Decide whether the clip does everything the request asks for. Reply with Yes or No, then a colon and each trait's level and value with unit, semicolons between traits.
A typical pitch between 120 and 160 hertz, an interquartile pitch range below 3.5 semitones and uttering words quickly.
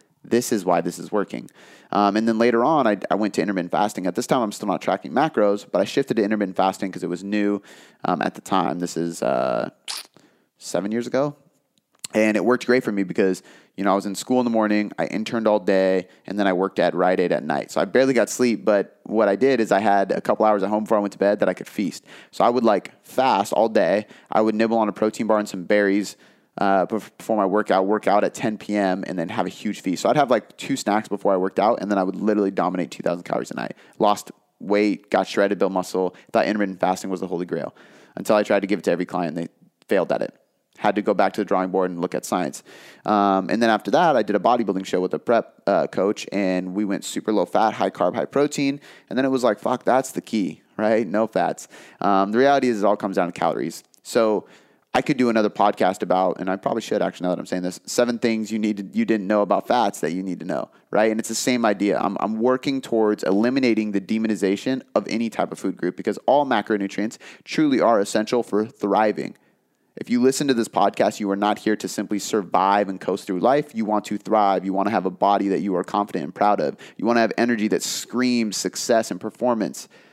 No: low, 105 Hz; narrow, 2.6 semitones; fast, 255 wpm